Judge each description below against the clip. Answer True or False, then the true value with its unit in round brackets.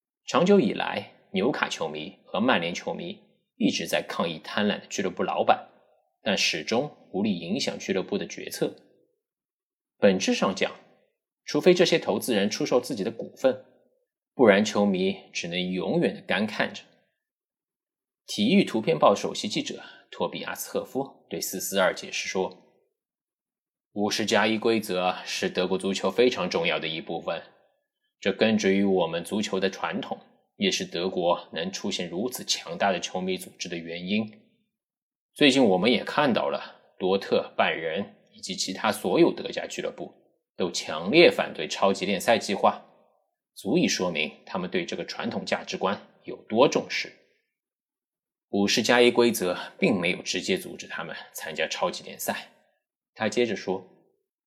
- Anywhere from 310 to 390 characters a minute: False (240 characters per minute)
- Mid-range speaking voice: True (175 Hz)